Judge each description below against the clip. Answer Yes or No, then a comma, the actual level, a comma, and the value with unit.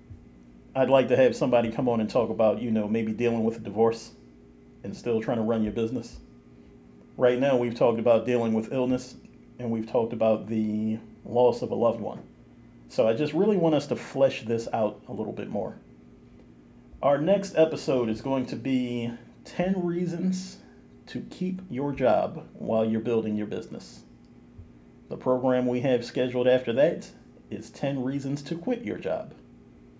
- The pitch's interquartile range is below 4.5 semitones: Yes, average, 3.7 semitones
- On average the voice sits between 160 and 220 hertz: No, low, 115 Hz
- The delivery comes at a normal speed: Yes, average, 175 wpm